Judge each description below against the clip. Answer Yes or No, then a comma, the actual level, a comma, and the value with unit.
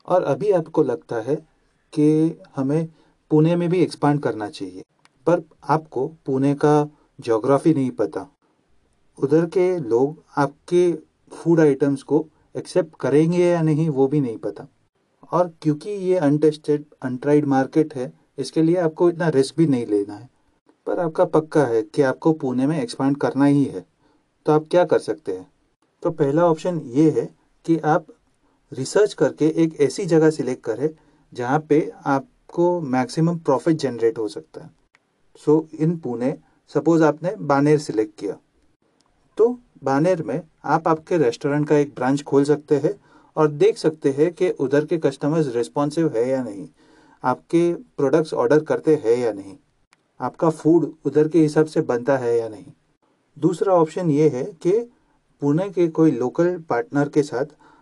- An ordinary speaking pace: Yes, average, 160 wpm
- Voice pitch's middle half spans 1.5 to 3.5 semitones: Yes, average, 2.7 semitones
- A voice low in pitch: No, medium, 150 Hz